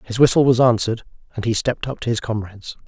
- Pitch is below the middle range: Yes, low, 115 Hz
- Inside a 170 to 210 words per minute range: No, fast, 230 wpm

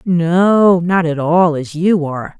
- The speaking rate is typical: Yes, average, 175 wpm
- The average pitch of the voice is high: No, medium, 170 Hz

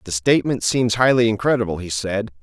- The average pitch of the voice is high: No, low, 110 Hz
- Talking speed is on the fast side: No, average, 175 wpm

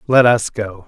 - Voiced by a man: Yes, male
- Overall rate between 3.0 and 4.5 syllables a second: Yes, 4.1 syllables/s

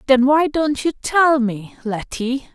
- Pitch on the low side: No, very high, 265 Hz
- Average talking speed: Yes, average, 165 wpm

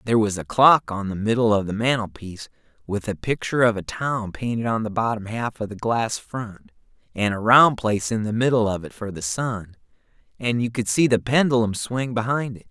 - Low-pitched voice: Yes, low, 110 Hz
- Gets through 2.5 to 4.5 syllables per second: No, 5.5 syllables/s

